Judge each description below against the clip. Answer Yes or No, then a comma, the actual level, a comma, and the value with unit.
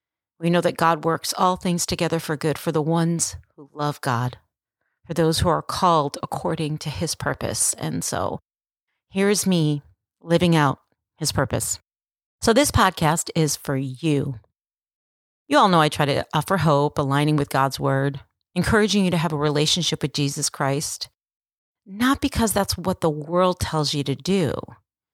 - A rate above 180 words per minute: No, average, 170 wpm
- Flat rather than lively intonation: No, average, 3.7 semitones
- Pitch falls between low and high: Yes, medium, 155 Hz